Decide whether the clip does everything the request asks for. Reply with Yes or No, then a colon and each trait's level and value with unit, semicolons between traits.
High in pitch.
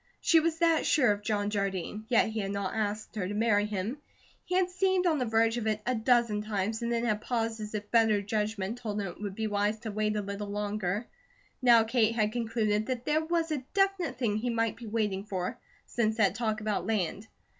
Yes: high, 220 Hz